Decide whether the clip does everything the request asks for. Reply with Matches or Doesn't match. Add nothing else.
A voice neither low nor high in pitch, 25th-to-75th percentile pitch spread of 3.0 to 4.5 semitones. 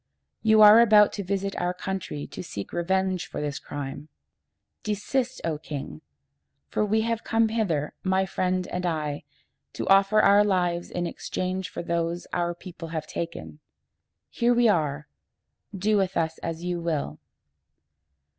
Matches